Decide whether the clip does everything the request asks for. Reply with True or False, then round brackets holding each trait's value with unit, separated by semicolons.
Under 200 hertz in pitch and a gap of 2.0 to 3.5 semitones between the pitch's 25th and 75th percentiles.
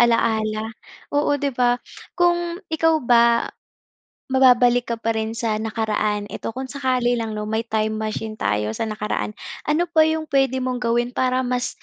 False (240 Hz; 3.1 semitones)